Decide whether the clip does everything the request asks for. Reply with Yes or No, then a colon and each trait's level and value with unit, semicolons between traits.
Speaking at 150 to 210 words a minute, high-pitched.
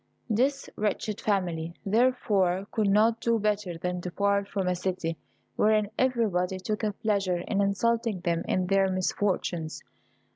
No: average, 140 wpm; high, 200 Hz